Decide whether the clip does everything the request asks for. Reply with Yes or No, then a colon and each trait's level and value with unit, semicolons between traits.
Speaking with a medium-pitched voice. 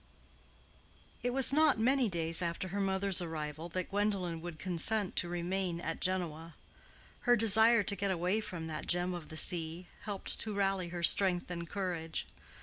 Yes: medium, 180 Hz